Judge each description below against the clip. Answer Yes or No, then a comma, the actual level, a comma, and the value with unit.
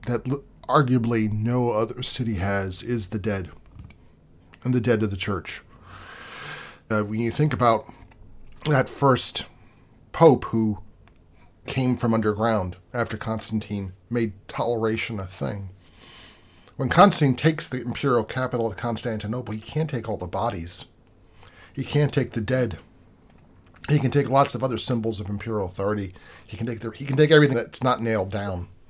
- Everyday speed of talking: Yes, average, 155 wpm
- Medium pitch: No, low, 115 Hz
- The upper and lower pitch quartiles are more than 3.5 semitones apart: Yes, average, 4.0 semitones